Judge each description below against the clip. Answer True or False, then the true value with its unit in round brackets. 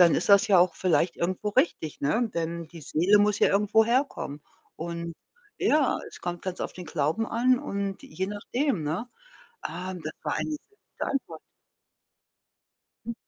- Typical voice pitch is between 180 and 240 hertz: True (185 Hz)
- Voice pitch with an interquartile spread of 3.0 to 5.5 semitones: True (4.8 semitones)